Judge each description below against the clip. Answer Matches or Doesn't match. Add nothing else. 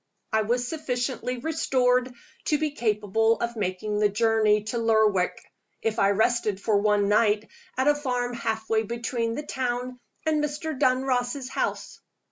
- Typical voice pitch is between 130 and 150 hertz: Doesn't match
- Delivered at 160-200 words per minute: Doesn't match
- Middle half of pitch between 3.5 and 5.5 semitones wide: Doesn't match